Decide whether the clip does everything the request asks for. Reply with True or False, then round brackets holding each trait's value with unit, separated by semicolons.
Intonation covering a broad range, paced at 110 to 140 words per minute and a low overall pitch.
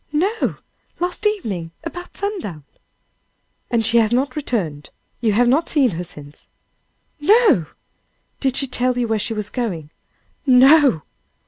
False (6.9 semitones; 135 wpm; 245 Hz)